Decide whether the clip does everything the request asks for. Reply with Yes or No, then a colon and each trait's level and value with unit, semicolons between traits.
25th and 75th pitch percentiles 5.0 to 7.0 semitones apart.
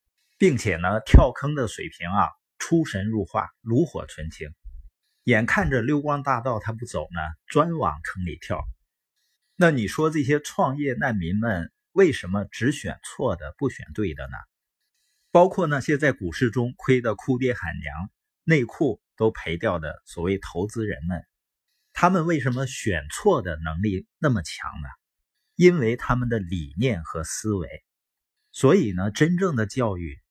No: wide, 8.1 semitones